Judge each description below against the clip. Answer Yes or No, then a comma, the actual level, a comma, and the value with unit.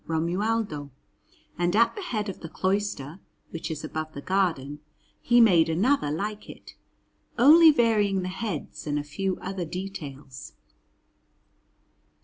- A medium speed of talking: No, slow, 130 wpm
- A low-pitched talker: No, medium, 185 Hz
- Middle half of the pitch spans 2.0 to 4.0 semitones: No, average, 5.1 semitones